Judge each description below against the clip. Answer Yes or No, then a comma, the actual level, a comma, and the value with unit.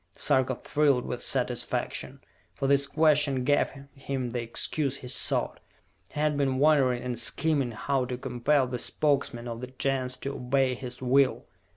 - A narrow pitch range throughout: Yes, narrow, 2.1 semitones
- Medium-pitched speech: No, low, 130 Hz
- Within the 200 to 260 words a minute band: No, average, 160 wpm